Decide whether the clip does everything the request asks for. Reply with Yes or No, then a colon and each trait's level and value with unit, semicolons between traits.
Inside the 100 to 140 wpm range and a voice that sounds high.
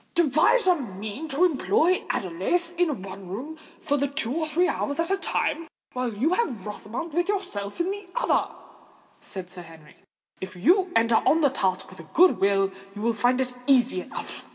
No: average, 180 wpm; very high, 265 Hz